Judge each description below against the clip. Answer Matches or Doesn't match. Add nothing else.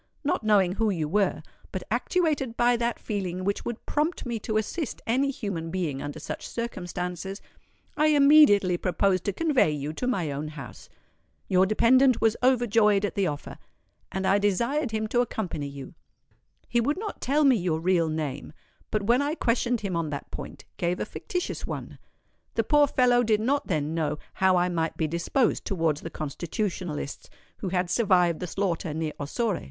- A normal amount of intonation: Doesn't match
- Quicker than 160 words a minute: Matches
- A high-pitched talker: Matches